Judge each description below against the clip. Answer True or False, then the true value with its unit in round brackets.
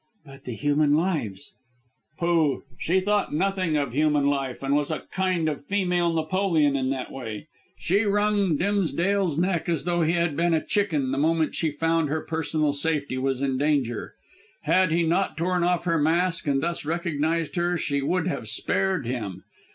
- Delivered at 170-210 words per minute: True (180 wpm)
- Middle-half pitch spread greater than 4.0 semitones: False (3.7 semitones)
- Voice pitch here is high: False (160 Hz)